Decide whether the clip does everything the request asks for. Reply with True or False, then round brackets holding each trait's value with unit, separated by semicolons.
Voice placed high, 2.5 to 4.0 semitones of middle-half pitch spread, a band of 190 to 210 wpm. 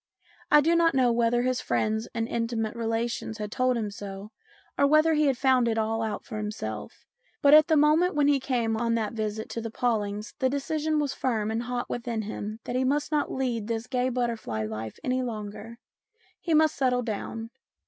True (235 Hz; 3.4 semitones; 205 wpm)